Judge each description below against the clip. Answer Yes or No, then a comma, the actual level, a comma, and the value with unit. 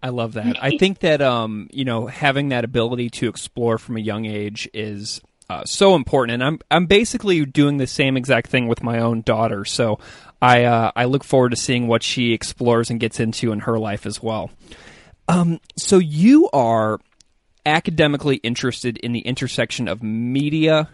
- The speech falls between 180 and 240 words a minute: Yes, average, 185 wpm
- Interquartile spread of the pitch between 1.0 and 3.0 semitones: No, average, 3.8 semitones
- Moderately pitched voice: No, low, 120 Hz